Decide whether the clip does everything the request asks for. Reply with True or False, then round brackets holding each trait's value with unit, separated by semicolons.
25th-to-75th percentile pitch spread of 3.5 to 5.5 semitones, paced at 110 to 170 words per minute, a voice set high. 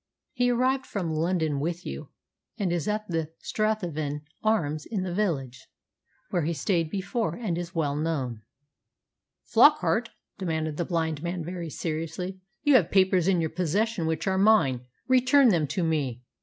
False (4.2 semitones; 155 wpm; 170 Hz)